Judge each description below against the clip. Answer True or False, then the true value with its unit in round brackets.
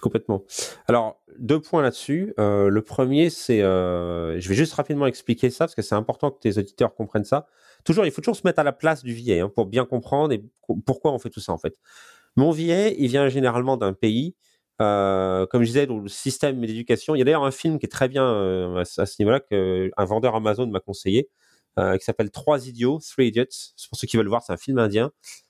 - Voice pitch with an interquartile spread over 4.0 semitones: True (5.1 semitones)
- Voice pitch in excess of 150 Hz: False (120 Hz)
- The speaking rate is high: True (235 wpm)